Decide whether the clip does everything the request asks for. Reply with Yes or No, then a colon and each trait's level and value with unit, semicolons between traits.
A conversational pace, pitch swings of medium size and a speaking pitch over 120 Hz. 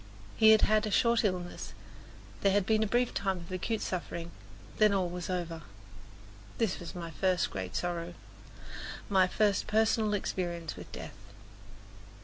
Yes: average, 150 wpm; average, 3.5 semitones; high, 190 Hz